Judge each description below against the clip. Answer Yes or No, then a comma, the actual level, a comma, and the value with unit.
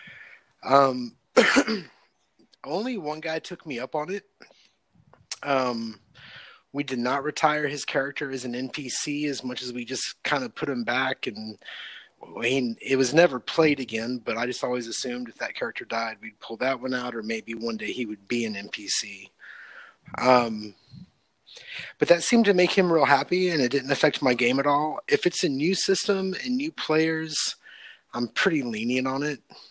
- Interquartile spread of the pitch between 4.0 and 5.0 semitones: Yes, average, 4.6 semitones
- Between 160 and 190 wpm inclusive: Yes, average, 180 wpm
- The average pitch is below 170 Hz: Yes, low, 135 Hz